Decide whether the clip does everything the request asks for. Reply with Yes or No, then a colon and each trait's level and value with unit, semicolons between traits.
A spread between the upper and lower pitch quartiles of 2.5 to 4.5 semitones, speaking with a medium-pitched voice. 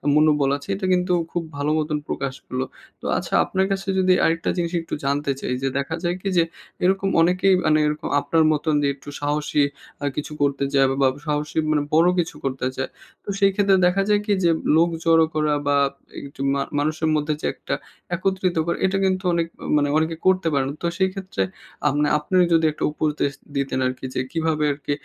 Yes: average, 3.7 semitones; medium, 155 Hz